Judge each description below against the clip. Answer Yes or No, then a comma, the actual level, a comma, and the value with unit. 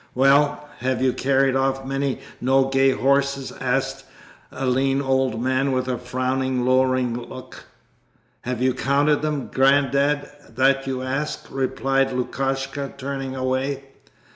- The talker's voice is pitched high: No, low, 135 Hz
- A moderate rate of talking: No, slow, 125 wpm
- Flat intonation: Yes, narrow, 1.0 semitones